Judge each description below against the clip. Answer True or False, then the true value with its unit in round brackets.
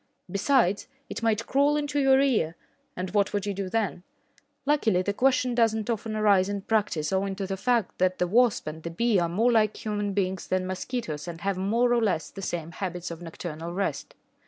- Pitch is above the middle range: True (200 Hz)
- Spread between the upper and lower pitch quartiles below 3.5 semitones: False (4.0 semitones)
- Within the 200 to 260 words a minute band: True (205 wpm)